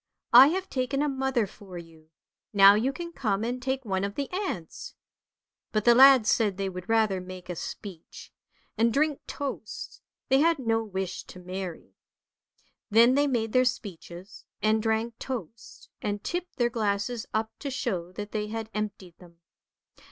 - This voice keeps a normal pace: Yes, average, 170 wpm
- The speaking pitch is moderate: No, high, 220 Hz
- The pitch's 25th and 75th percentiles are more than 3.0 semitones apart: Yes, average, 4.8 semitones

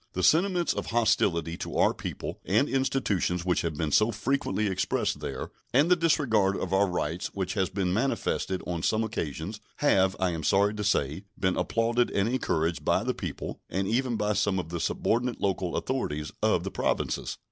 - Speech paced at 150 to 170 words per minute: No, average, 185 wpm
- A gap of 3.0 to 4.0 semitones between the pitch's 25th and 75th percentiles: No, average, 4.7 semitones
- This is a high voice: No, low, 100 Hz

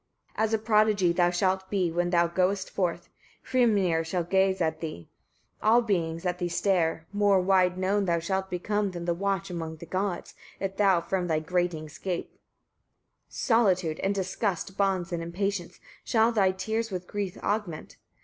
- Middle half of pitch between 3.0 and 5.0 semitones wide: No, narrow, 2.5 semitones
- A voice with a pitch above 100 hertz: Yes, medium, 185 Hz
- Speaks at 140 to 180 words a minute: Yes, average, 170 wpm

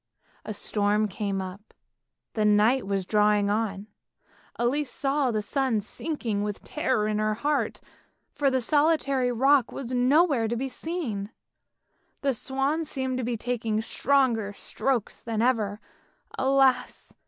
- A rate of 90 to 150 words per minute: Yes, slow, 135 wpm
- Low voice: No, high, 240 Hz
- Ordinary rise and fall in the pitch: Yes, average, 4.3 semitones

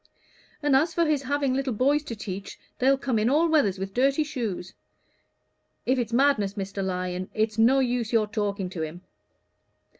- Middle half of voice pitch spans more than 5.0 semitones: Yes, wide, 5.5 semitones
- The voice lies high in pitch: Yes, high, 235 Hz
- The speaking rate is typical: Yes, average, 175 wpm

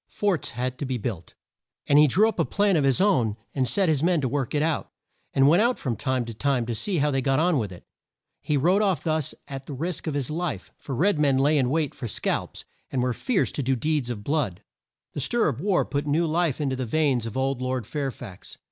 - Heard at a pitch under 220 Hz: Yes, medium, 140 Hz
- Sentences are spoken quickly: Yes, fast, 250 wpm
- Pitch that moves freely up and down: No, average, 4.0 semitones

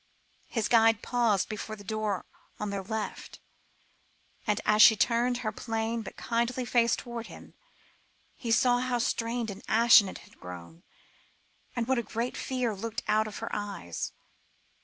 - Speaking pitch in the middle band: No, high, 225 Hz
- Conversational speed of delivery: Yes, average, 160 wpm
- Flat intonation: Yes, narrow, 2.1 semitones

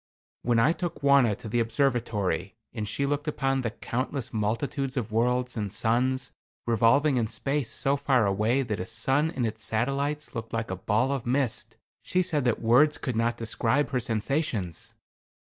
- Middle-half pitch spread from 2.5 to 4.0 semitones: Yes, average, 3.6 semitones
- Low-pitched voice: Yes, low, 120 Hz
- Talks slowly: No, average, 175 wpm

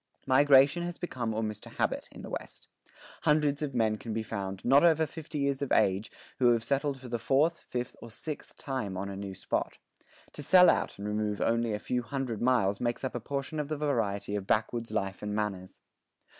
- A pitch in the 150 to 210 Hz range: No, low, 120 Hz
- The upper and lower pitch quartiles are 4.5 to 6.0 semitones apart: Yes, average, 5.0 semitones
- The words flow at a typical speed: No, fast, 210 wpm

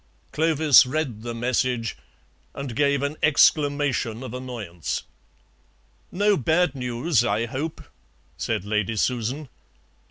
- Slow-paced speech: Yes, slow, 105 wpm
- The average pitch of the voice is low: Yes, low, 130 Hz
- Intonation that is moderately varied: Yes, average, 4.2 semitones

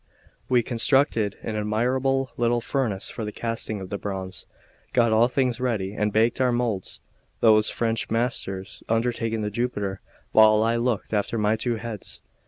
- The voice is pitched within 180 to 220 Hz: No, low, 115 Hz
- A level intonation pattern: Yes, narrow, 2.3 semitones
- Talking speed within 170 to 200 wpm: No, average, 160 wpm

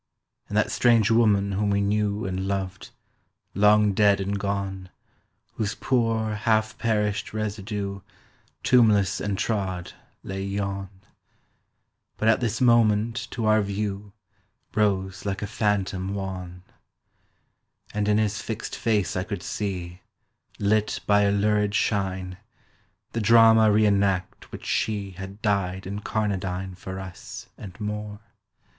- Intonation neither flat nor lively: No, narrow, 1.8 semitones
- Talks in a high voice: No, low, 100 Hz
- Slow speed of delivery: Yes, slow, 125 wpm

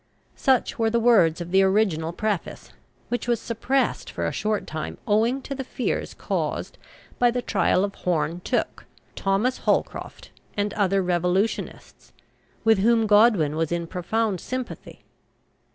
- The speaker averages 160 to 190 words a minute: No, average, 145 wpm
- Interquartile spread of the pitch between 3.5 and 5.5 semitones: Yes, average, 4.7 semitones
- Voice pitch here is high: Yes, high, 205 Hz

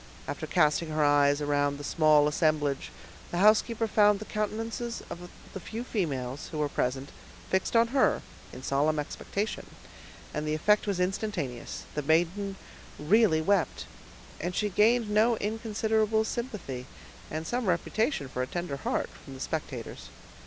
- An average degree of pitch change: No, wide, 6.5 semitones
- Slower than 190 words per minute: Yes, average, 150 wpm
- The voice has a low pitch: No, medium, 175 Hz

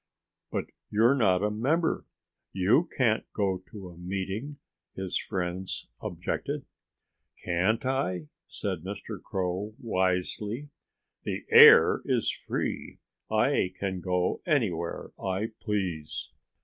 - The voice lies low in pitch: Yes, very low, 95 Hz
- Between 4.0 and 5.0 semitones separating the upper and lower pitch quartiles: No, average, 3.4 semitones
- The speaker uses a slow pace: Yes, slow, 110 wpm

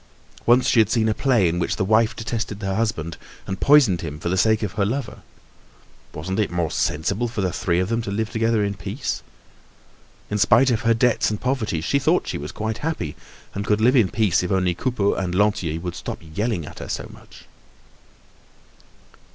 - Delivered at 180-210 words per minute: Yes, fast, 205 wpm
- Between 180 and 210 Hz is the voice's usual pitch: No, low, 105 Hz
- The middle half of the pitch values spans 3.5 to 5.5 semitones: Yes, average, 4.0 semitones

